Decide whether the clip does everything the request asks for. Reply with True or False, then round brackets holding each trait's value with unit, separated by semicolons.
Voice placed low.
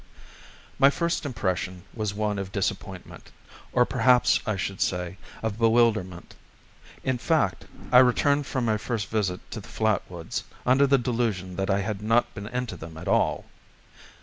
True (110 Hz)